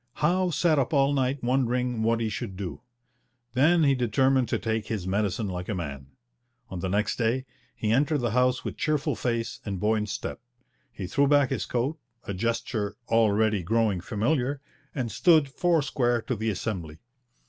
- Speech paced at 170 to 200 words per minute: Yes, average, 175 wpm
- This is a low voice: Yes, low, 115 Hz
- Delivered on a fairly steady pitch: No, average, 4.5 semitones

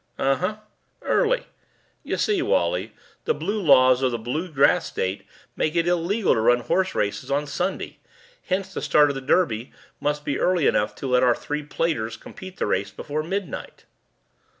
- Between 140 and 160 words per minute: No, average, 170 wpm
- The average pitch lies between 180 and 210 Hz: No, medium, 150 Hz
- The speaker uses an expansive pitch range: Yes, wide, 6.3 semitones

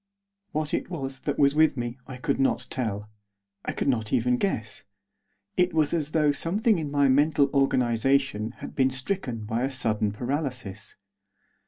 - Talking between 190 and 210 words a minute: No, average, 165 wpm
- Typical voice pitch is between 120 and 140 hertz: Yes, low, 135 Hz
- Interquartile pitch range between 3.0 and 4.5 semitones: Yes, average, 3.7 semitones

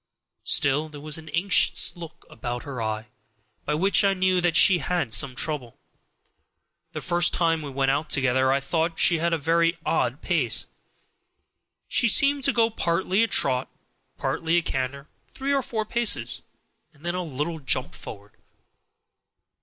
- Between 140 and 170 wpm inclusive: Yes, average, 160 wpm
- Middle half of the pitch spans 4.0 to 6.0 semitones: Yes, average, 4.9 semitones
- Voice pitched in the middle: Yes, medium, 160 Hz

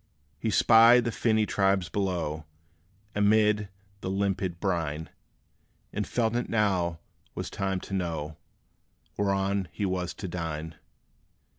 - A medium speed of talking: No, slow, 120 wpm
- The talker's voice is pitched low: Yes, very low, 95 Hz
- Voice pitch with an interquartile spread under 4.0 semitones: Yes, average, 3.4 semitones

